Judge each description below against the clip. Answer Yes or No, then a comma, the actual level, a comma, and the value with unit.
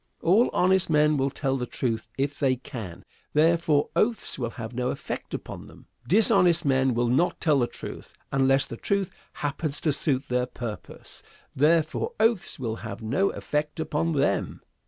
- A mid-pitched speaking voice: Yes, medium, 145 Hz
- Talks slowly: No, average, 165 wpm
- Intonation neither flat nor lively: Yes, average, 4.6 semitones